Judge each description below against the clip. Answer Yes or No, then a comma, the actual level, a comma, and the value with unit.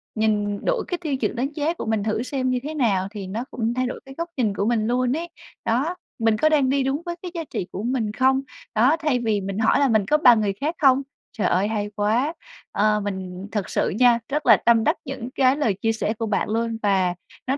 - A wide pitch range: No, average, 4.4 semitones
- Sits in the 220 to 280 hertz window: Yes, high, 235 Hz